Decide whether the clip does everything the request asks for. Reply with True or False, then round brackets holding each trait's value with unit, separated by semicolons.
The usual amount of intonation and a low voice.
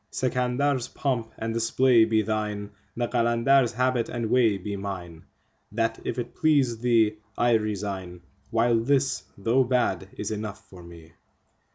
True (3.0 semitones; 115 Hz)